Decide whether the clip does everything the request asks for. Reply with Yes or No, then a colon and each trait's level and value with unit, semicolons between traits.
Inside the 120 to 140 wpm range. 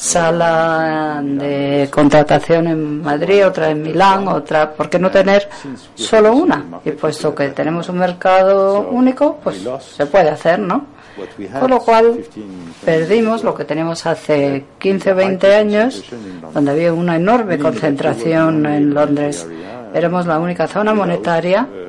Yes: average, 135 wpm